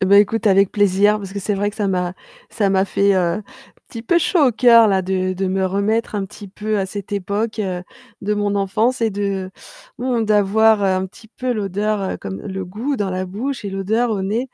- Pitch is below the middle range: No, high, 205 Hz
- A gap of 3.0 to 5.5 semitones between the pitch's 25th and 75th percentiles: No, narrow, 2.4 semitones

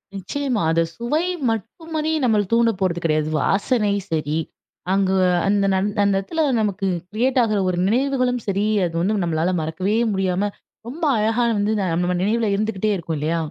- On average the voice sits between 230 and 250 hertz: No, high, 205 Hz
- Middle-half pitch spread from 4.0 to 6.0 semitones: Yes, average, 4.4 semitones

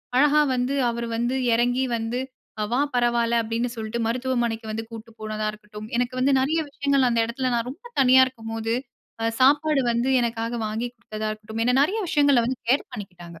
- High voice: Yes, high, 240 Hz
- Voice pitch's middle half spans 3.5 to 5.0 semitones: No, narrow, 2.5 semitones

